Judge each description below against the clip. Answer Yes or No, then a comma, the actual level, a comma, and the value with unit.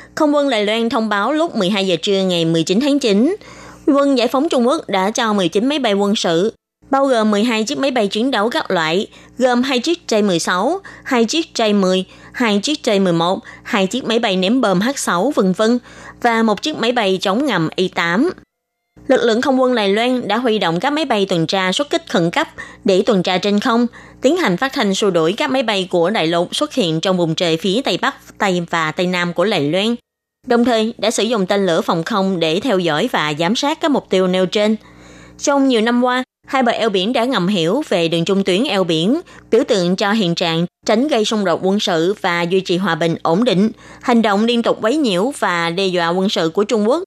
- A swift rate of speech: No, average, 230 wpm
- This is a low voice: No, high, 210 Hz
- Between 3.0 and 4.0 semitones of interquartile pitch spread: No, average, 5.0 semitones